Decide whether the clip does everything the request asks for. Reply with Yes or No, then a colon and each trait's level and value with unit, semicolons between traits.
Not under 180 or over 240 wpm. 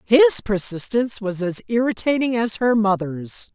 No: slow, 135 wpm